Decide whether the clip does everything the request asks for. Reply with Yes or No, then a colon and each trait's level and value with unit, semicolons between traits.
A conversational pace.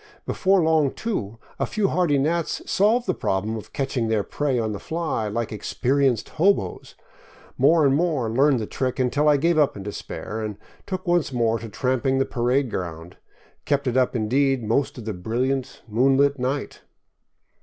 Yes: average, 175 wpm